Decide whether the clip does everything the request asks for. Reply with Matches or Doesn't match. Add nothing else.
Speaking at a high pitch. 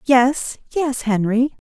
Matches